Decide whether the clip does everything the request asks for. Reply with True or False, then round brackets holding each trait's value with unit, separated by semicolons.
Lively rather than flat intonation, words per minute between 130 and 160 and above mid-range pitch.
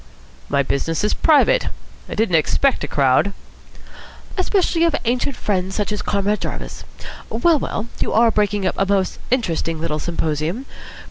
True (7.2 semitones; 150 wpm; 205 Hz)